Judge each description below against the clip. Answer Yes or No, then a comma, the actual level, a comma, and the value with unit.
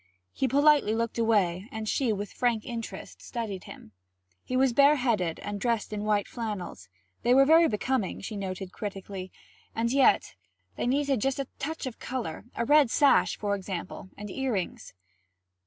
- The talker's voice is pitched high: Yes, high, 225 Hz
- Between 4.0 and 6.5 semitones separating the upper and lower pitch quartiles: Yes, average, 4.7 semitones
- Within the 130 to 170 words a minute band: Yes, average, 160 wpm